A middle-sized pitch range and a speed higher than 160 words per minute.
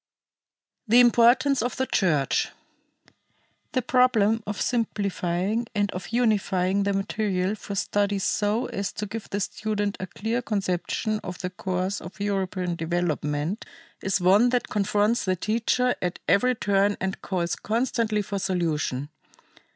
No: average, 3.3 semitones; slow, 135 wpm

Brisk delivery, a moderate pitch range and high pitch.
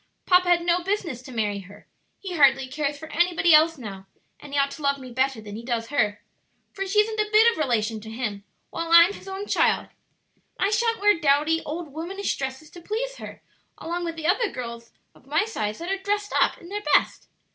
No: fast, 220 wpm; wide, 6.9 semitones; very high, 315 Hz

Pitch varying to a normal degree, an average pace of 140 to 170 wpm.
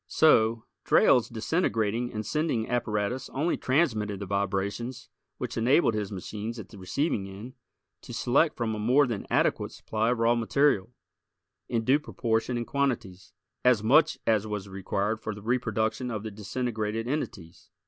Yes: average, 3.2 semitones; average, 155 wpm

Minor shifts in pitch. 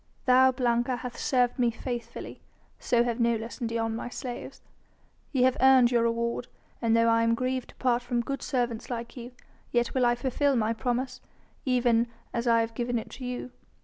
Yes: narrow, 1.4 semitones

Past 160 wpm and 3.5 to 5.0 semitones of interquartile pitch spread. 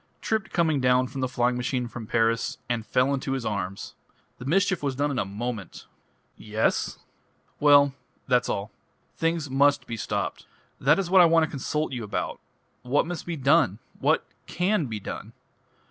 Yes: average, 175 wpm; average, 4.5 semitones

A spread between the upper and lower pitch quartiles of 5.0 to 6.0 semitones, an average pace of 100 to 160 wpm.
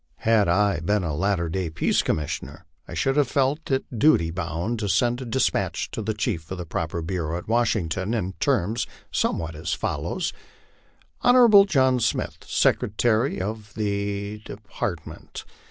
Yes: wide, 5.6 semitones; average, 155 wpm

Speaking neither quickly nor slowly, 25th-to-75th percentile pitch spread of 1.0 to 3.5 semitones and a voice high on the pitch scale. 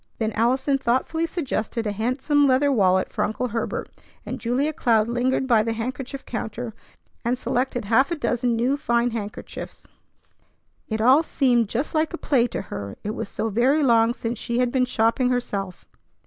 Yes: average, 175 wpm; average, 2.8 semitones; high, 245 Hz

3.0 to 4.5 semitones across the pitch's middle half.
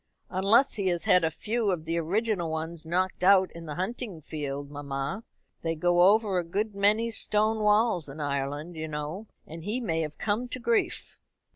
No: average, 5.0 semitones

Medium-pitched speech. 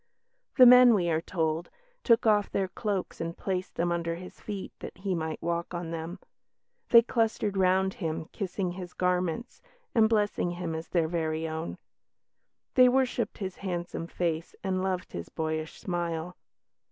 Yes: medium, 180 Hz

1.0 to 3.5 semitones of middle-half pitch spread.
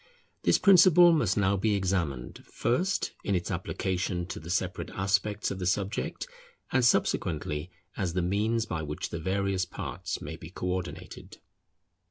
Yes: average, 3.2 semitones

